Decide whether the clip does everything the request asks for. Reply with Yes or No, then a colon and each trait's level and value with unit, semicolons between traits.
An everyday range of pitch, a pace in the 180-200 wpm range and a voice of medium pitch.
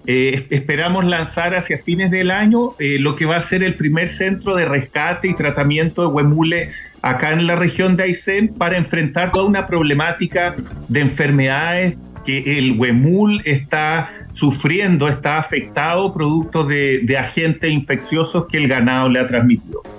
No: average, 3.9 semitones; average, 160 wpm; medium, 160 Hz